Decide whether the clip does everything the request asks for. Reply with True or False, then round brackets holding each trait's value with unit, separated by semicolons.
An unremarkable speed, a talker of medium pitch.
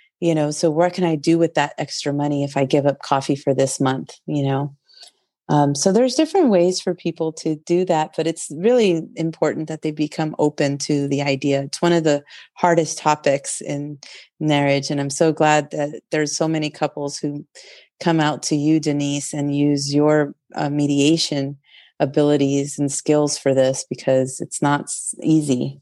True (185 wpm; 150 Hz)